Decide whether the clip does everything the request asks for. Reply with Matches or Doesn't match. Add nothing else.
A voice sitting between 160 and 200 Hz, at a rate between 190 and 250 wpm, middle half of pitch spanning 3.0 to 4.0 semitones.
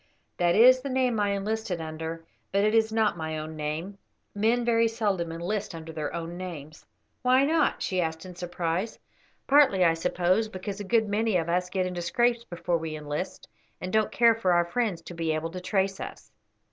Doesn't match